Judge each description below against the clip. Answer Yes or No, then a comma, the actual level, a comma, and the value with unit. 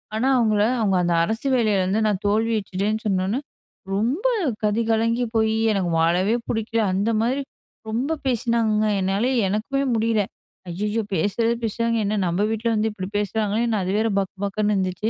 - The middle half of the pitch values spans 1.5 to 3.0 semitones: Yes, narrow, 2.5 semitones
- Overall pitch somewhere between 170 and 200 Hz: No, high, 215 Hz